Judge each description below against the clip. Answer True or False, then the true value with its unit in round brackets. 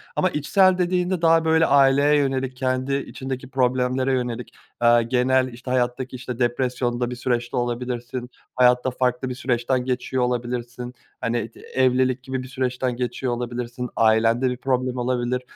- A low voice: True (125 Hz)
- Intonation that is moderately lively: False (1.3 semitones)